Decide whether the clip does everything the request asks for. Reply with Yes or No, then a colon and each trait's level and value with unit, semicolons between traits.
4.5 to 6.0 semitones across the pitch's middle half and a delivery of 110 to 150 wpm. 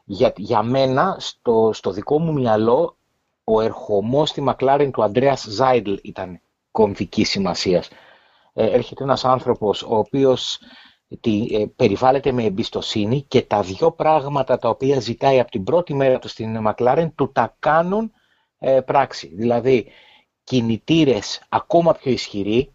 No: average, 3.8 semitones; average, 140 wpm